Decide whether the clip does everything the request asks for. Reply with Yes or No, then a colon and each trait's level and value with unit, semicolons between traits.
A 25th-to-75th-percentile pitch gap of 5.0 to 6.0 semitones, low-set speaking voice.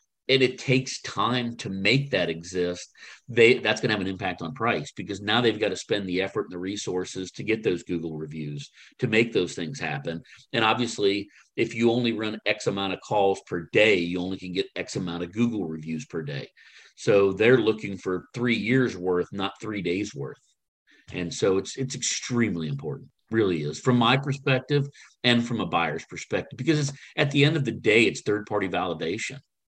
Yes: average, 5.3 semitones; low, 105 Hz